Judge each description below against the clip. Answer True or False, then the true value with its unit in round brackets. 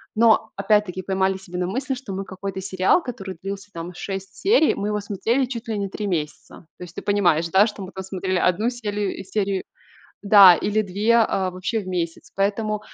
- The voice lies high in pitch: True (195 Hz)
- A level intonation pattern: True (2.2 semitones)